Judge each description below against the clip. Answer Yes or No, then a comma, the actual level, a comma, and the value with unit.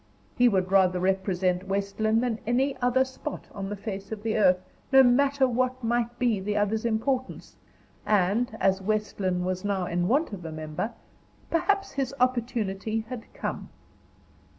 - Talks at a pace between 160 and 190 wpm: Yes, average, 165 wpm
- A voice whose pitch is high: Yes, high, 215 Hz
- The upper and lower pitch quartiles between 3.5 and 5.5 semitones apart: Yes, average, 4.4 semitones